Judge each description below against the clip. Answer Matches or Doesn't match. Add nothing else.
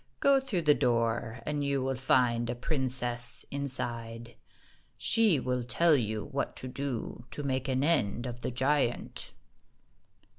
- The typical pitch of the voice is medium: Doesn't match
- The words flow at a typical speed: Matches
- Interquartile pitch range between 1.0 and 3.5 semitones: Matches